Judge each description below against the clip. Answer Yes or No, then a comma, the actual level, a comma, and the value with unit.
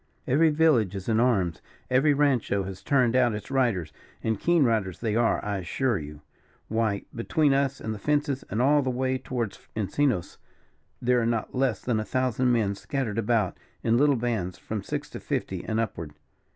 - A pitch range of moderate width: Yes, average, 4.2 semitones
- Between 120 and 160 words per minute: No, average, 185 wpm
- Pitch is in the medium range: No, low, 120 Hz